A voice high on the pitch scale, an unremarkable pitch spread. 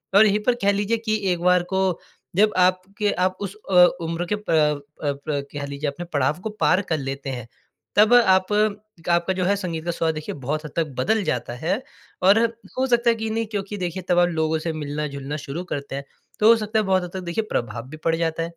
No: medium, 175 Hz; average, 4.9 semitones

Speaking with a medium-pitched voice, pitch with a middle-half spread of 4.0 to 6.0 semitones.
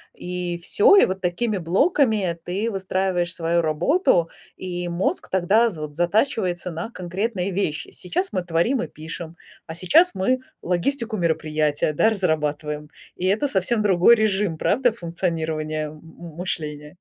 Yes: medium, 180 Hz; average, 4.3 semitones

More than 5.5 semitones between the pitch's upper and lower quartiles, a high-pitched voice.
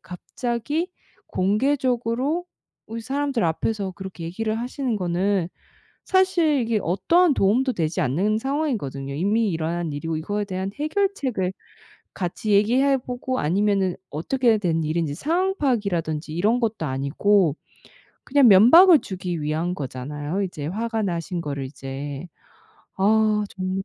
Yes: wide, 6.9 semitones; high, 200 Hz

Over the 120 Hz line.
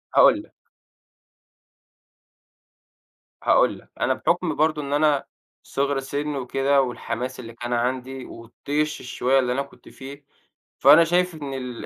Yes: low, 135 Hz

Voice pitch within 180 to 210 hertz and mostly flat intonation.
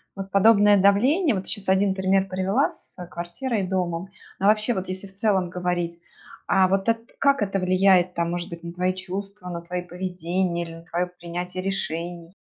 Yes: medium, 185 Hz; narrow, 2.0 semitones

